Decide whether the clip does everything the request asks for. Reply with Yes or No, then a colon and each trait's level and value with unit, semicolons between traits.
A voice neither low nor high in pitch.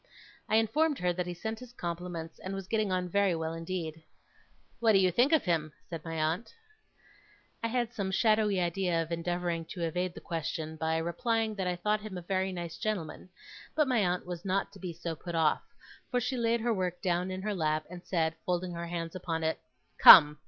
Yes: medium, 180 Hz